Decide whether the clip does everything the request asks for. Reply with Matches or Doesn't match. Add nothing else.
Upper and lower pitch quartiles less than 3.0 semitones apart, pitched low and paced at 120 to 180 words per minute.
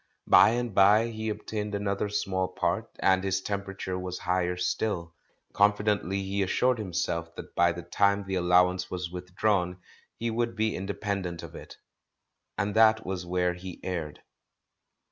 Matches